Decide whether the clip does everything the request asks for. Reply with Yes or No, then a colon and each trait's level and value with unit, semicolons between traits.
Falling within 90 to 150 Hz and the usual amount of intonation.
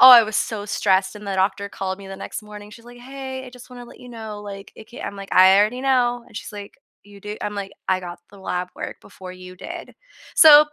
No: high, 210 Hz; average, 3.9 semitones